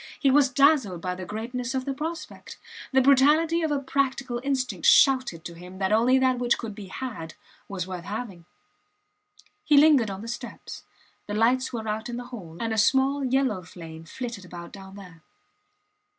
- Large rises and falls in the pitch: Yes, wide, 5.7 semitones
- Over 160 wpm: Yes, average, 180 wpm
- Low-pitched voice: No, high, 240 Hz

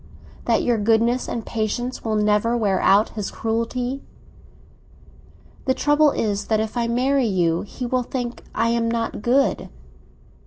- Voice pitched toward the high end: Yes, high, 230 Hz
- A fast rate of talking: No, average, 150 wpm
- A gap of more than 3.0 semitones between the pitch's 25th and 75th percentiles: No, narrow, 2.5 semitones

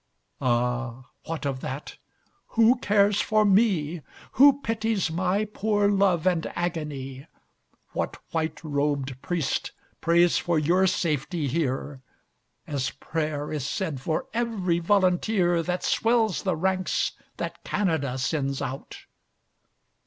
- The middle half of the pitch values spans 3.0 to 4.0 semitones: No, wide, 5.6 semitones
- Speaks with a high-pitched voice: No, medium, 170 Hz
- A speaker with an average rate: No, slow, 115 wpm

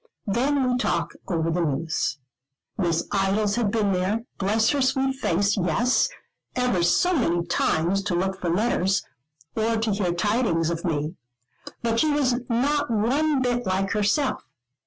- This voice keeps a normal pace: Yes, average, 155 wpm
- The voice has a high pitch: Yes, high, 205 Hz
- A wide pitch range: Yes, wide, 6.0 semitones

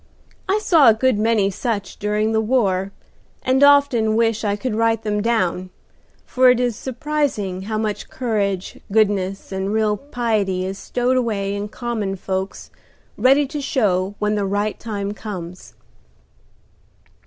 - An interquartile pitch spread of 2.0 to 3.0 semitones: No, average, 3.5 semitones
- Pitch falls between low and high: No, high, 215 Hz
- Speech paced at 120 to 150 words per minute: Yes, average, 145 wpm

